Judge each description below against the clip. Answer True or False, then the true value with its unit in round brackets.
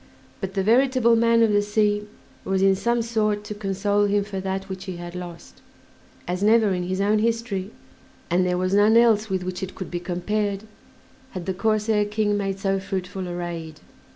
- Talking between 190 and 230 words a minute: True (195 wpm)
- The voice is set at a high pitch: True (200 Hz)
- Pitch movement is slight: True (2.3 semitones)